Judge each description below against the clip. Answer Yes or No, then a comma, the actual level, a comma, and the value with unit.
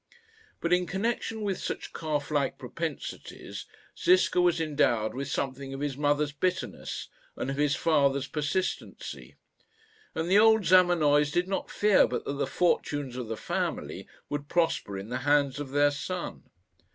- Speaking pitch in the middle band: Yes, medium, 145 Hz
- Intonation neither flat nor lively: Yes, average, 4.2 semitones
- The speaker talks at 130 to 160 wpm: Yes, average, 155 wpm